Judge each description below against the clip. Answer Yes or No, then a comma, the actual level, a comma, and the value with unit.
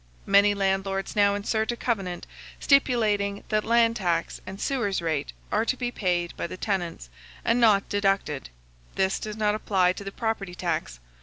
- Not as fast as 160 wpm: No, average, 165 wpm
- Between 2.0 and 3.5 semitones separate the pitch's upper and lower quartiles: Yes, average, 3.0 semitones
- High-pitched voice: Yes, high, 200 Hz